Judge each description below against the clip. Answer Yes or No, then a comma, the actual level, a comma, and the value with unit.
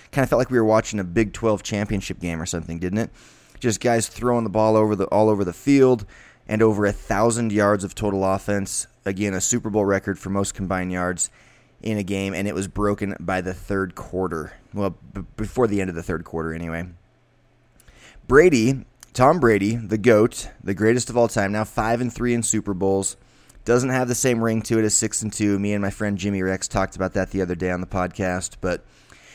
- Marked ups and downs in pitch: No, average, 2.7 semitones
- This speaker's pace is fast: Yes, fast, 225 wpm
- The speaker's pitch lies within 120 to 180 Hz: No, low, 100 Hz